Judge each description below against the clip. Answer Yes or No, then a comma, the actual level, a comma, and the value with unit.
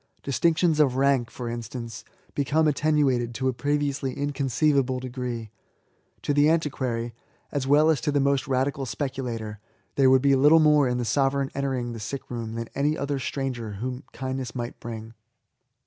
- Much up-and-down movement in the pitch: No, average, 2.9 semitones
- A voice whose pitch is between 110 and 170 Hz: Yes, low, 135 Hz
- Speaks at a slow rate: No, average, 165 wpm